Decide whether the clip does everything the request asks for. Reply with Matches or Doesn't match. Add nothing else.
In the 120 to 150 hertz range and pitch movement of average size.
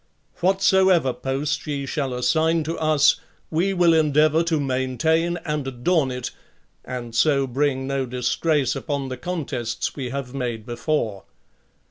Matches